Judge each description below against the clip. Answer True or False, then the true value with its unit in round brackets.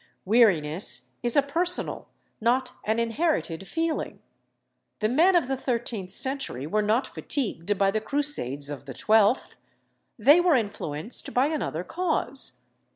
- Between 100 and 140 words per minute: True (135 wpm)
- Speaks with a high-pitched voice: True (235 Hz)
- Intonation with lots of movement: True (6.1 semitones)